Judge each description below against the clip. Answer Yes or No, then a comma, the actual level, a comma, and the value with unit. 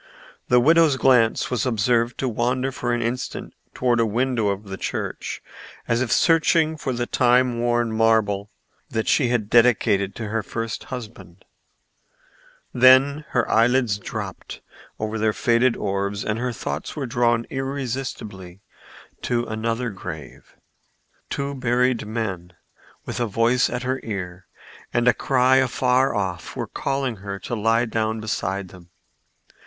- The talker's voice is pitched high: No, low, 115 Hz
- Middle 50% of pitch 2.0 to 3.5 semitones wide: Yes, average, 3.1 semitones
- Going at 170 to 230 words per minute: No, average, 145 wpm